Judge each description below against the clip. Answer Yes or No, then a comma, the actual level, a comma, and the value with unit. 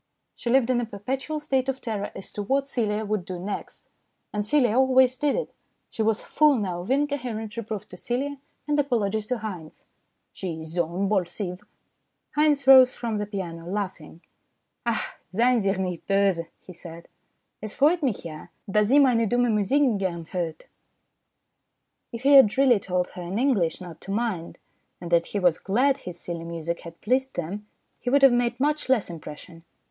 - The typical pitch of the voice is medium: No, high, 210 Hz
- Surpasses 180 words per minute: Yes, average, 190 wpm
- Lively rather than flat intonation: Yes, wide, 6.1 semitones